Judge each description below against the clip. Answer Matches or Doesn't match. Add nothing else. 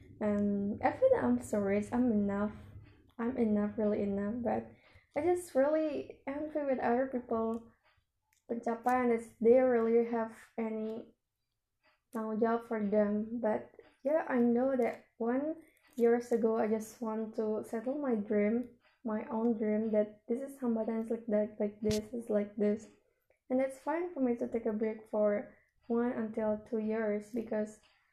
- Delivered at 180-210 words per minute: Doesn't match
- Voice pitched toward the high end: Matches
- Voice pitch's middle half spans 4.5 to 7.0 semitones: Doesn't match